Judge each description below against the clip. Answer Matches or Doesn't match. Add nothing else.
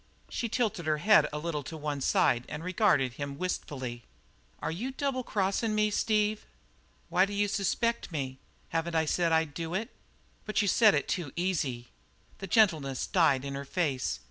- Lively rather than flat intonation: Matches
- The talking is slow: Doesn't match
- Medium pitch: Matches